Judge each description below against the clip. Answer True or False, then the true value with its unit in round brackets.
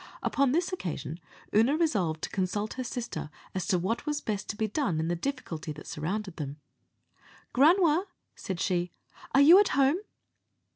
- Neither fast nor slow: True (165 wpm)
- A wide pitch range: True (8.4 semitones)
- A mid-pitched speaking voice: False (215 Hz)